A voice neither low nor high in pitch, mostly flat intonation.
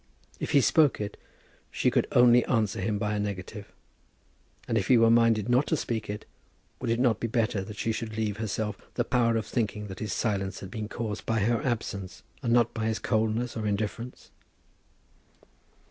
No: low, 110 Hz; narrow, 2.1 semitones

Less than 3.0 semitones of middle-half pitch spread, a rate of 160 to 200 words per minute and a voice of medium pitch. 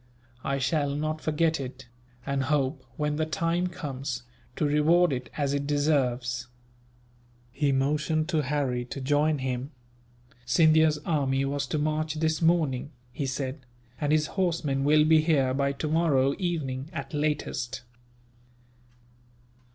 No: narrow, 2.6 semitones; slow, 135 wpm; medium, 145 Hz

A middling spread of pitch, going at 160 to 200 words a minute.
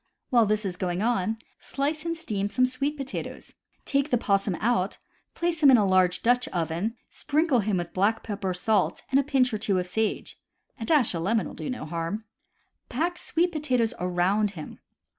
No: wide, 6.1 semitones; average, 190 wpm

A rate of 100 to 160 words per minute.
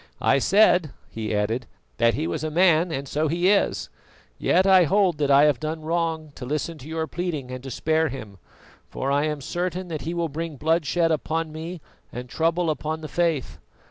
No: average, 200 wpm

